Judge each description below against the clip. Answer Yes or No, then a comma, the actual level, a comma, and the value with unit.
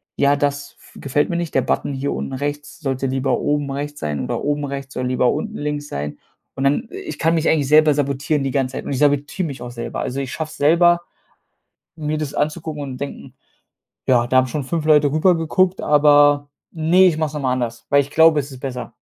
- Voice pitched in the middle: Yes, medium, 145 Hz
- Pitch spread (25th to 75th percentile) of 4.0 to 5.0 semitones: No, narrow, 2.5 semitones